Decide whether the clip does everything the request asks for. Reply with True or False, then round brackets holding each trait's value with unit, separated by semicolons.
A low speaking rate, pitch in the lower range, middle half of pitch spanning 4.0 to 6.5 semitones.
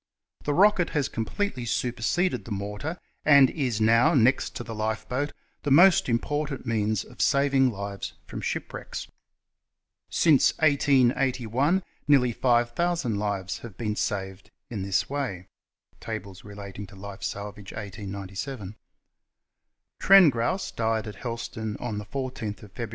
True (130 wpm; 115 Hz; 5.1 semitones)